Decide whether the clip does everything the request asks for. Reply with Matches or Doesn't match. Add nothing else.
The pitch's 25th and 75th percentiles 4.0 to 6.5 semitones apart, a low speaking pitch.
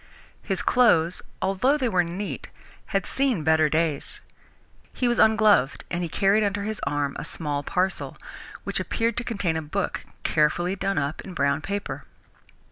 Doesn't match